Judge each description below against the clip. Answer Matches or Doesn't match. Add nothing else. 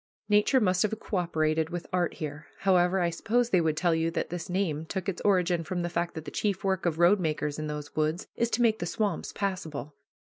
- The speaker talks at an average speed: Doesn't match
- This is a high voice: Doesn't match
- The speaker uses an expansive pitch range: Doesn't match